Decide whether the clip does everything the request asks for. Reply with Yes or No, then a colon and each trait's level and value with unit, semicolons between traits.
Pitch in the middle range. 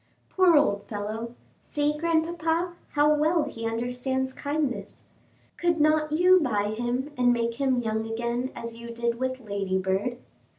No: very high, 250 Hz